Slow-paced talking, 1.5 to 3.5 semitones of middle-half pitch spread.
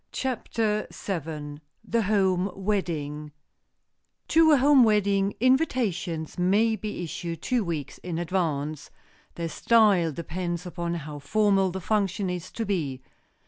No: slow, 125 wpm; average, 4.5 semitones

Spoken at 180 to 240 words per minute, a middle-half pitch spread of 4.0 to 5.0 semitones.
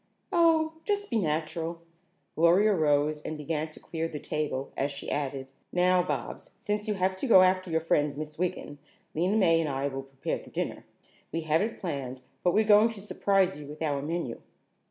Yes: average, 195 wpm; average, 4.4 semitones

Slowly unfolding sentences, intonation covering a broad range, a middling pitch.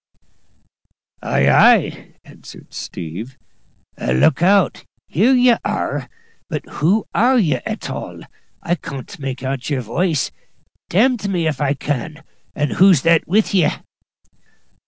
Yes: slow, 130 wpm; wide, 6.5 semitones; medium, 160 Hz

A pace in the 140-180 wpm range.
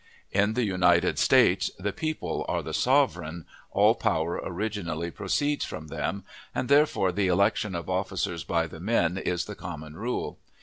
Yes: average, 160 wpm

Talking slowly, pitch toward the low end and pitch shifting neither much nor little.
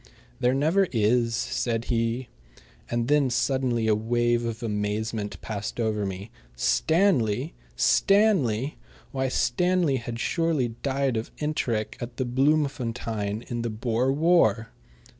Yes: slow, 120 wpm; low, 120 Hz; average, 3.5 semitones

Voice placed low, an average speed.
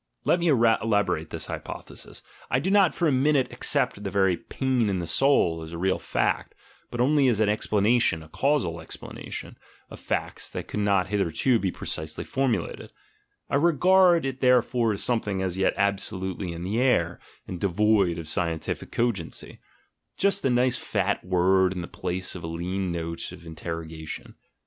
Yes: low, 100 Hz; average, 180 wpm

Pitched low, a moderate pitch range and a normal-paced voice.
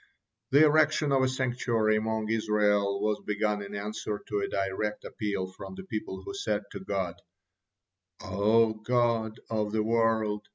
No: low, 110 Hz; narrow, 2.0 semitones; average, 160 wpm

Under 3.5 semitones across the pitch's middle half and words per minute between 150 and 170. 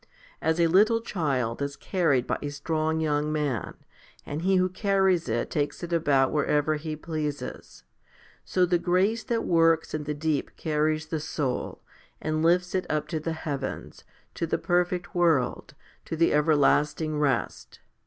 Yes: average, 2.9 semitones; average, 160 wpm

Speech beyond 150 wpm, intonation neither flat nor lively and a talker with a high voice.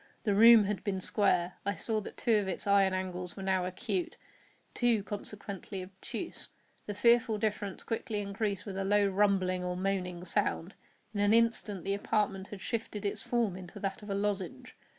No: average, 175 wpm; narrow, 1.9 semitones; high, 200 Hz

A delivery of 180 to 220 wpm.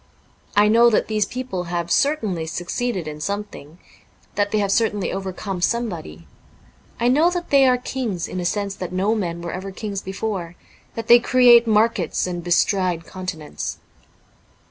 No: average, 160 wpm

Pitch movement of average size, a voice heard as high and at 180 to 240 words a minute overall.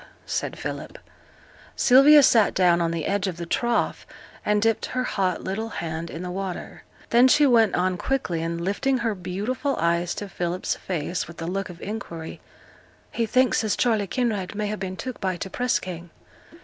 Yes: average, 5.0 semitones; high, 195 Hz; average, 185 wpm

